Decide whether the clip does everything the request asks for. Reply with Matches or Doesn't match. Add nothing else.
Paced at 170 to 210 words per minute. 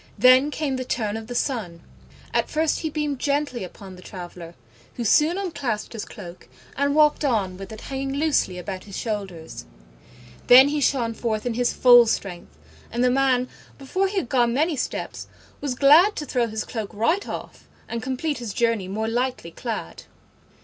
Matches